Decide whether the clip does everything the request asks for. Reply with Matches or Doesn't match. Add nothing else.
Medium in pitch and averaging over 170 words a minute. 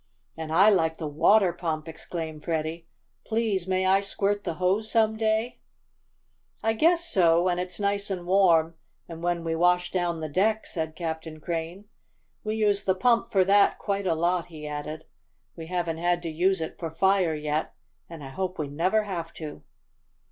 Matches